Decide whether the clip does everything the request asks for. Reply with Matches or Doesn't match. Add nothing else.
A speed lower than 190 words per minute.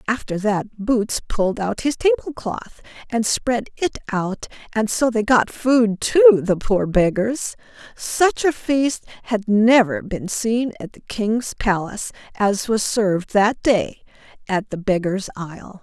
Matches